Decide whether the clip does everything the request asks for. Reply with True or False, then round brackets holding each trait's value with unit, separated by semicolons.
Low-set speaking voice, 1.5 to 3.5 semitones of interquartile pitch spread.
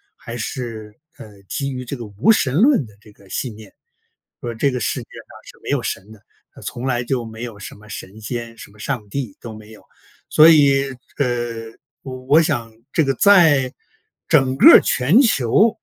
False (120 Hz; 4.0 semitones)